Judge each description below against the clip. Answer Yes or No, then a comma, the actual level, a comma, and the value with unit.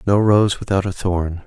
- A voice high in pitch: No, very low, 95 Hz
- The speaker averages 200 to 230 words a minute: Yes, fast, 205 wpm